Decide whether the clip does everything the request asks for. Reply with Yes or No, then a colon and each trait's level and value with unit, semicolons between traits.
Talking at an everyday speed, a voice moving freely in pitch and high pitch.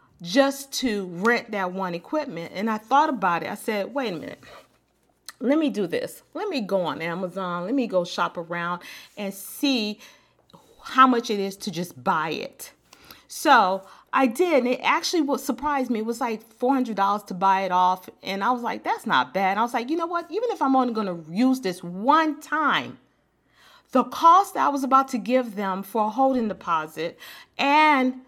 Yes: average, 195 wpm; wide, 6.3 semitones; high, 230 Hz